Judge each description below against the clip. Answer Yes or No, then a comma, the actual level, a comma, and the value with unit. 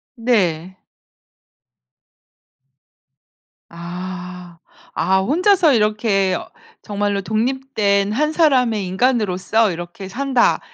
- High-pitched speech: Yes, high, 205 Hz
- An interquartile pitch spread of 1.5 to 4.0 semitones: No, average, 5.1 semitones